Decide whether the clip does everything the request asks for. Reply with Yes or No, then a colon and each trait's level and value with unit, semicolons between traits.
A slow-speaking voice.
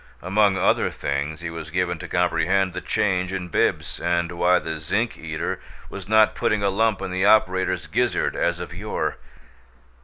No: average, 175 wpm